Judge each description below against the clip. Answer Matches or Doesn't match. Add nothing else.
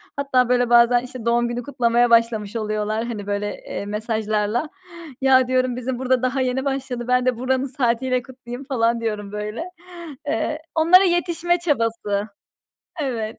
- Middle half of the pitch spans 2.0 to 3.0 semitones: Matches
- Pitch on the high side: Matches